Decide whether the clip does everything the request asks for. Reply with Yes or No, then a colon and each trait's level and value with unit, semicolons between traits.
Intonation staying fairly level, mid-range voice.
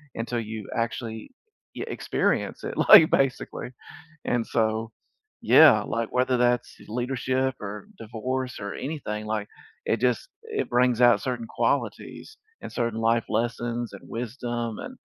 No: narrow, 2.1 semitones; low, 120 Hz